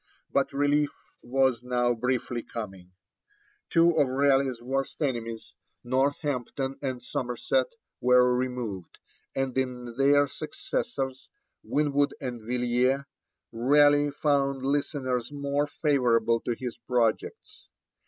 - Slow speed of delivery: Yes, slow, 105 wpm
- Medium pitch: No, low, 130 Hz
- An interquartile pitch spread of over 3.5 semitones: No, narrow, 2.6 semitones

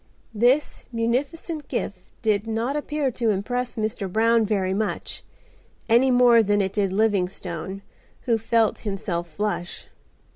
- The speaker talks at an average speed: No, slow, 130 wpm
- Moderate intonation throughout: Yes, average, 3.5 semitones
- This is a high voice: Yes, high, 220 Hz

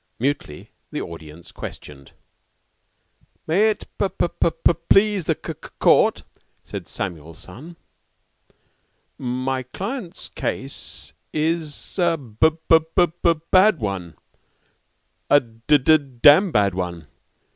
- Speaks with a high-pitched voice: No, medium, 140 Hz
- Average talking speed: No, slow, 105 wpm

